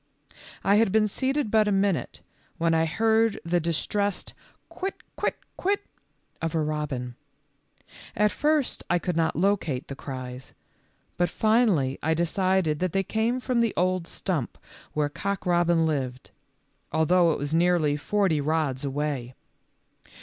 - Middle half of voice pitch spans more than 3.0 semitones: Yes, average, 5.2 semitones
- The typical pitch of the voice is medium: Yes, medium, 175 Hz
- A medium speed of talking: Yes, average, 155 wpm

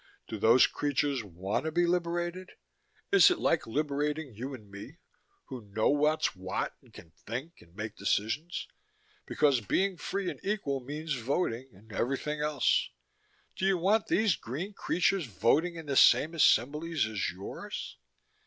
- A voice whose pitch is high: No, medium, 145 Hz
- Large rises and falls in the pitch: Yes, wide, 7.1 semitones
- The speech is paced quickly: No, average, 155 wpm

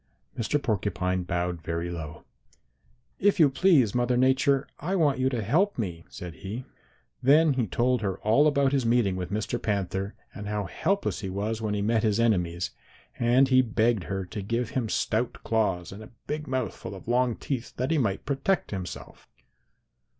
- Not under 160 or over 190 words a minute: Yes, average, 180 wpm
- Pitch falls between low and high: No, low, 115 Hz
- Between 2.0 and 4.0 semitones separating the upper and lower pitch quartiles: No, average, 5.3 semitones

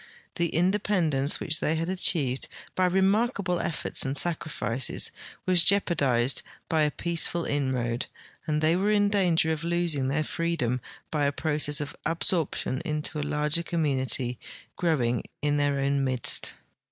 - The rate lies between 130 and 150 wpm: Yes, average, 145 wpm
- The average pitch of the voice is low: No, medium, 155 Hz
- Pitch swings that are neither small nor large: Yes, average, 3.7 semitones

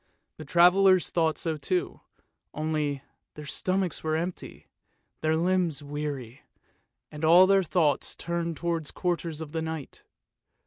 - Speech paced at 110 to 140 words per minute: Yes, slow, 135 wpm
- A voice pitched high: No, medium, 160 Hz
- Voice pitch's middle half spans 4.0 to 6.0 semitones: No, average, 2.7 semitones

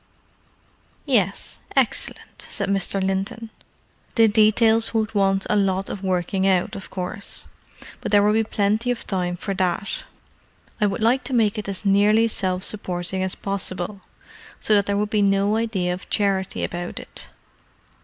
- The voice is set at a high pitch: Yes, high, 200 Hz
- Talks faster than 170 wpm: No, average, 155 wpm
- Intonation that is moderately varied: No, narrow, 2.2 semitones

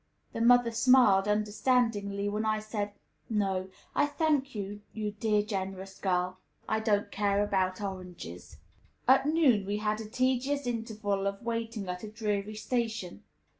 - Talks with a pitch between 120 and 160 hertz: No, high, 210 Hz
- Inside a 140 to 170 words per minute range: Yes, average, 150 wpm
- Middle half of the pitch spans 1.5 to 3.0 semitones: Yes, average, 2.7 semitones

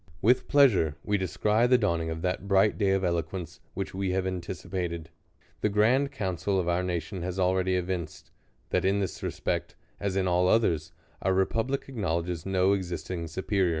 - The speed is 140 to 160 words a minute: No, average, 175 wpm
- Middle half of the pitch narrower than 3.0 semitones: Yes, narrow, 2.4 semitones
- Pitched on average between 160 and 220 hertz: No, very low, 95 Hz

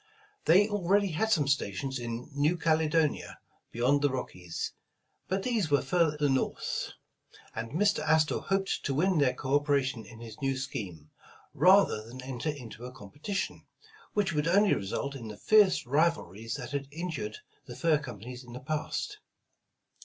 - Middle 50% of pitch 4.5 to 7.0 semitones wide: Yes, wide, 5.4 semitones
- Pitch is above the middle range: No, medium, 145 Hz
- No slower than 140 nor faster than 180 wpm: Yes, average, 160 wpm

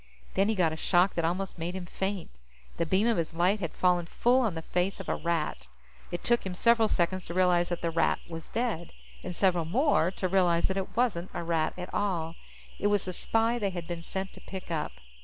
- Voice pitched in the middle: Yes, medium, 180 Hz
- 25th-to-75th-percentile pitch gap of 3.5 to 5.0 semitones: No, narrow, 2.6 semitones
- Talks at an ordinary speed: No, fast, 230 wpm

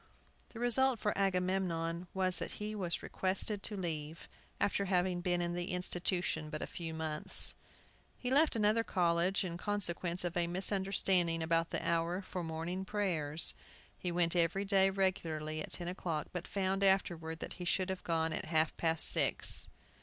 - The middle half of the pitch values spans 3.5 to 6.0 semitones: No, narrow, 2.6 semitones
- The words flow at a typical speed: Yes, average, 170 wpm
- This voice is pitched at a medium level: Yes, medium, 180 Hz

